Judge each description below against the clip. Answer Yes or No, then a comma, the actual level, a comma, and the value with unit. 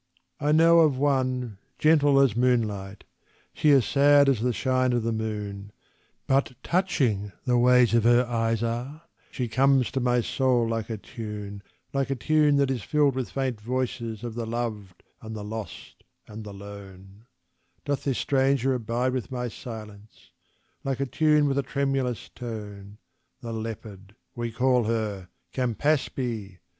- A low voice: Yes, low, 120 Hz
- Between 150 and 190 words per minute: Yes, average, 155 wpm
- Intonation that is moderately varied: Yes, average, 3.6 semitones